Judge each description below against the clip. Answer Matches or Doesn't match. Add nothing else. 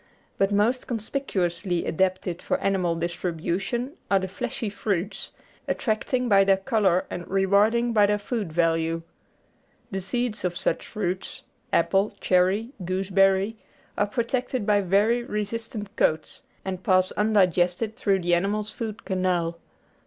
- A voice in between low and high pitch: Doesn't match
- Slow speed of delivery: Matches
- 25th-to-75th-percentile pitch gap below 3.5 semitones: Matches